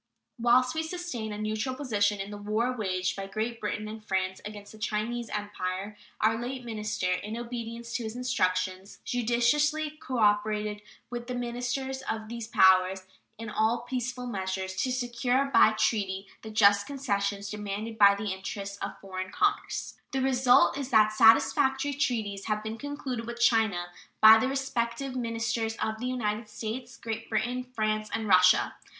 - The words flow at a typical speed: Yes, average, 160 wpm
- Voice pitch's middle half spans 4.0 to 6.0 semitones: No, average, 3.1 semitones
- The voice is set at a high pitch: Yes, high, 220 Hz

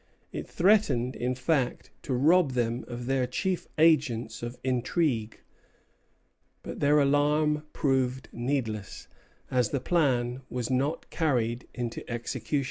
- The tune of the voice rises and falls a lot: No, average, 3.6 semitones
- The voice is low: Yes, low, 130 Hz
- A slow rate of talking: Yes, slow, 125 wpm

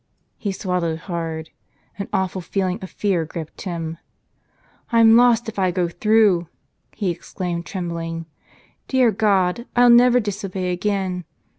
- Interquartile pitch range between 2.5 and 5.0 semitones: Yes, average, 3.8 semitones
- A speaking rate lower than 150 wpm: Yes, slow, 135 wpm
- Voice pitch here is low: No, medium, 185 Hz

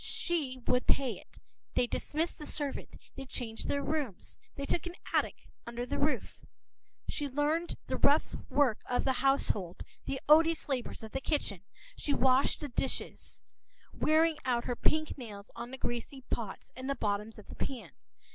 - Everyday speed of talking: Yes, average, 170 wpm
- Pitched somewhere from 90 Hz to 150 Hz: No, very high, 270 Hz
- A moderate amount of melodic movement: Yes, average, 3.6 semitones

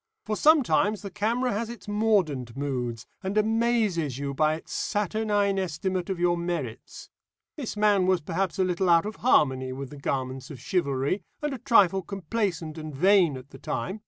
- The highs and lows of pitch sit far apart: Yes, wide, 6.3 semitones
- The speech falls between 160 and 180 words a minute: Yes, average, 175 wpm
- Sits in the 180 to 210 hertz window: Yes, medium, 185 Hz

